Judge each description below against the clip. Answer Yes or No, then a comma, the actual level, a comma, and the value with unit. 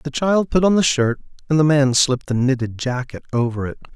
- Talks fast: Yes, fast, 230 wpm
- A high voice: No, medium, 140 Hz